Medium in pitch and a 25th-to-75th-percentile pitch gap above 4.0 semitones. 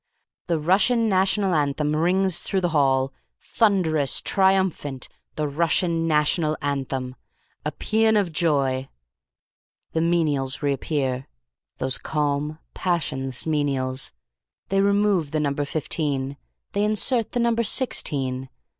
Yes: medium, 155 Hz; average, 5.3 semitones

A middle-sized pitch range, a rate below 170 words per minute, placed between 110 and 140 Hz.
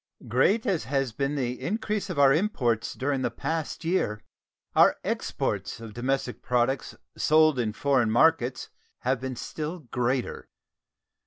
Yes: average, 4.3 semitones; average, 140 wpm; low, 135 Hz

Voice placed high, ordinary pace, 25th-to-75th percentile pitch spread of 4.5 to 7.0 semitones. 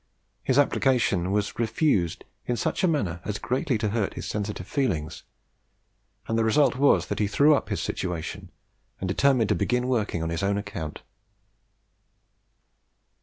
No: low, 110 Hz; average, 155 wpm; average, 5.2 semitones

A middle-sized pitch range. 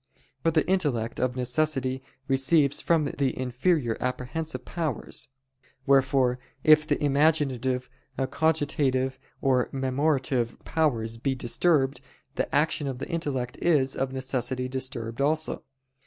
Yes: average, 3.2 semitones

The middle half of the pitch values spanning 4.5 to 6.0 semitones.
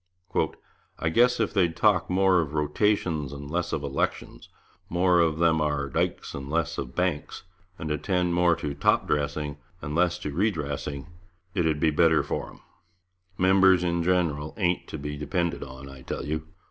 No: average, 3.4 semitones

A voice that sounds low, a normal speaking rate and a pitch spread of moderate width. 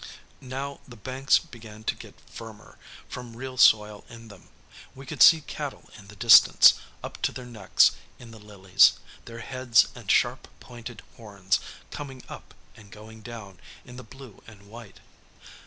Yes: low, 115 Hz; average, 160 wpm; average, 3.3 semitones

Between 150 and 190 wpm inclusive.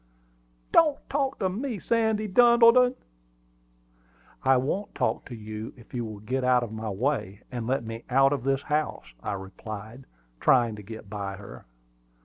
Yes: average, 160 wpm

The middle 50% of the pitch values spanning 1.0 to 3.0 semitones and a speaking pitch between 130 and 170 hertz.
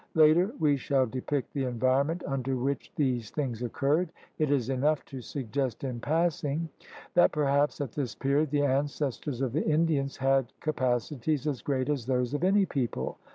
Yes: average, 2.7 semitones; medium, 140 Hz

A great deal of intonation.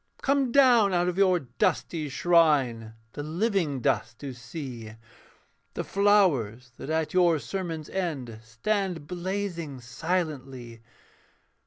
Yes: wide, 6.5 semitones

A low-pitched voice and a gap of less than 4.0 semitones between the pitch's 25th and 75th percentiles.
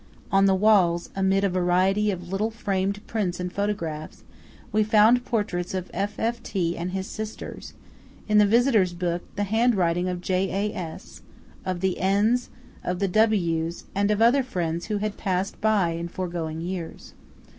No: high, 195 Hz; average, 3.1 semitones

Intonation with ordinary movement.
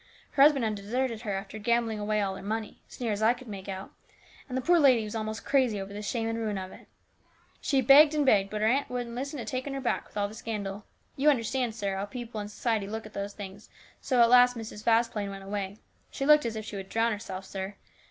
Yes: average, 3.4 semitones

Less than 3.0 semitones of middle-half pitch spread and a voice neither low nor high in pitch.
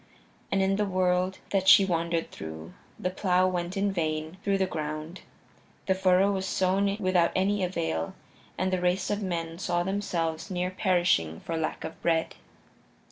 Yes: narrow, 2.4 semitones; medium, 180 Hz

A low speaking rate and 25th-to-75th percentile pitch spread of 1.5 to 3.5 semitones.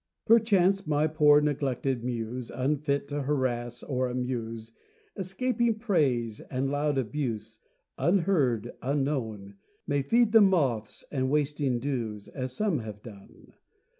No: slow, 120 wpm; average, 4.2 semitones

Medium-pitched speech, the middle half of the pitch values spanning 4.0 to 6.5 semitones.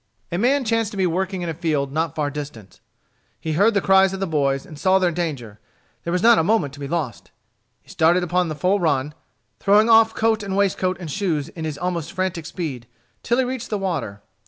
Yes: medium, 175 Hz; average, 4.6 semitones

